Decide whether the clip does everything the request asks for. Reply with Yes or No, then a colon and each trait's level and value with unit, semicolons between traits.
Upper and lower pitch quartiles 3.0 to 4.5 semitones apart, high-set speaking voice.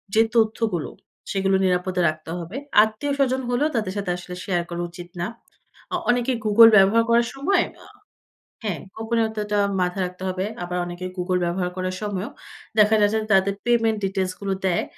Yes: average, 3.8 semitones; high, 200 Hz